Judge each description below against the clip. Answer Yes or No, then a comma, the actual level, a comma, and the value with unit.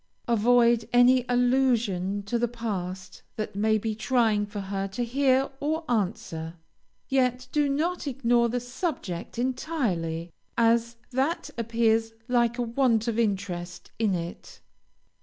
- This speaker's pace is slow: Yes, slow, 130 wpm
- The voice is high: Yes, high, 235 Hz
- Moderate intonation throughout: Yes, average, 3.5 semitones